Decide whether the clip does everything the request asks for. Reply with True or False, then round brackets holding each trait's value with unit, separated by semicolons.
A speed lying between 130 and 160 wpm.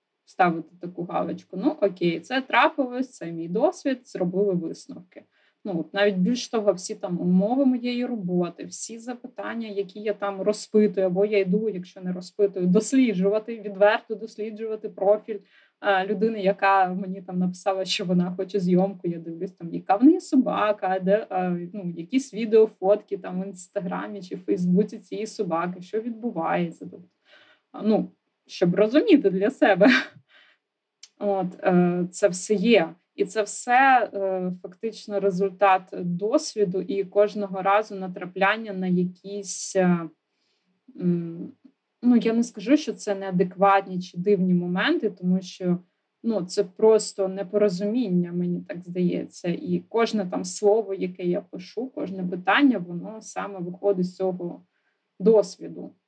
True (135 wpm)